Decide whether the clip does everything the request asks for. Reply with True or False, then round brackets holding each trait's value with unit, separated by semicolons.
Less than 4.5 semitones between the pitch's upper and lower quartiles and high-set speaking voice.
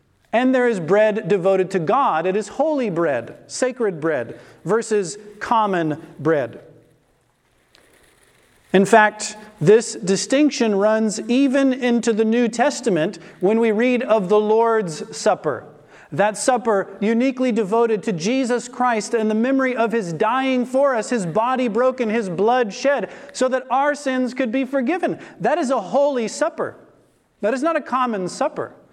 True (3.6 semitones; 230 Hz)